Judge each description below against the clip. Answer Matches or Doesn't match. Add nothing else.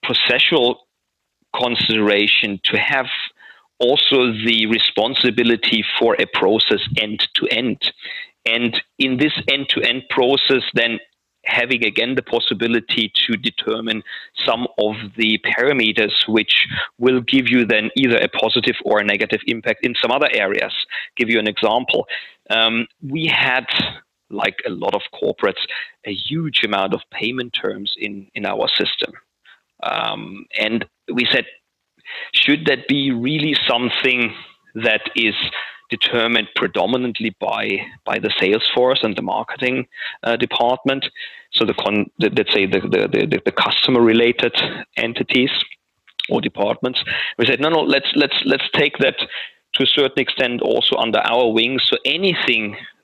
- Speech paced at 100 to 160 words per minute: Matches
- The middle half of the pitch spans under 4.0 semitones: Matches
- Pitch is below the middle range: Matches